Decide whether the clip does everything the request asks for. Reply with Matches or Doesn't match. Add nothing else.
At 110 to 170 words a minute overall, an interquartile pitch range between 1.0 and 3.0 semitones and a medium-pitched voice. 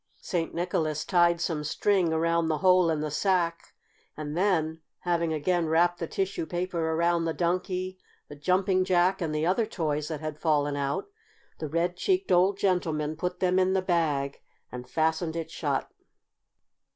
Matches